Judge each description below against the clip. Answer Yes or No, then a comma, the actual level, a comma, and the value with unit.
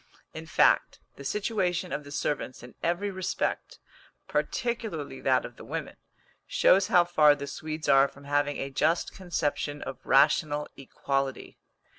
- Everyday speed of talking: Yes, average, 145 wpm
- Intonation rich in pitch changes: No, average, 3.9 semitones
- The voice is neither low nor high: Yes, medium, 150 Hz